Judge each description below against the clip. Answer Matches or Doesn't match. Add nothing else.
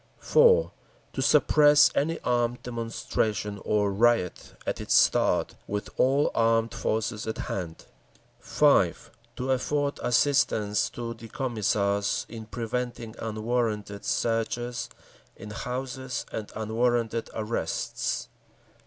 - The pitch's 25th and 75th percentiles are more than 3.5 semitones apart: Doesn't match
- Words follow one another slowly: Matches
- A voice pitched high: Doesn't match